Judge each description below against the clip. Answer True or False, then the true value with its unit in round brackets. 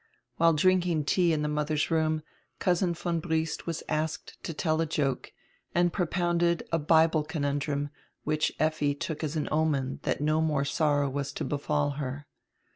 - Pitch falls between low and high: True (155 Hz)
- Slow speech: False (165 wpm)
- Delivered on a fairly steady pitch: True (2.1 semitones)